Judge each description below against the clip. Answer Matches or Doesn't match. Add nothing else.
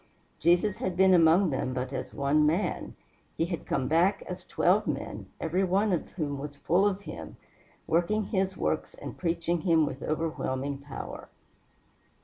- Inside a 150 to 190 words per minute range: Matches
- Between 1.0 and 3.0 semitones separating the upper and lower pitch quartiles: Doesn't match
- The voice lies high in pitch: Doesn't match